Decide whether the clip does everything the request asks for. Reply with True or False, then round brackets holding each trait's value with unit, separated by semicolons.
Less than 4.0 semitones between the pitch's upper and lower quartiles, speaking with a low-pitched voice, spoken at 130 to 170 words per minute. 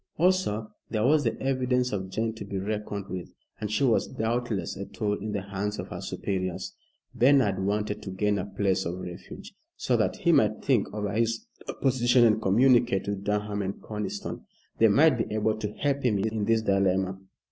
False (2.9 semitones; 105 Hz; 190 wpm)